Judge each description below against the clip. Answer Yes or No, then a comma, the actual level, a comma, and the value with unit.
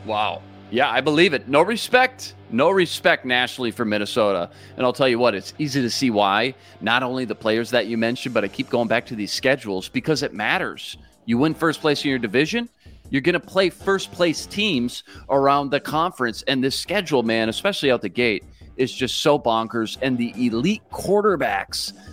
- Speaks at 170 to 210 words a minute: Yes, average, 200 wpm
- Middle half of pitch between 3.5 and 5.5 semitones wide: Yes, average, 4.7 semitones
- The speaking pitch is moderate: No, low, 125 Hz